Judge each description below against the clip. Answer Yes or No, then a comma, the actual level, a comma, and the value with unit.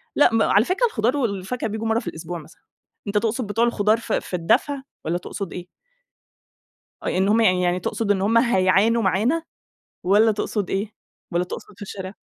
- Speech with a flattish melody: No, average, 3.5 semitones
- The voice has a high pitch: Yes, high, 210 Hz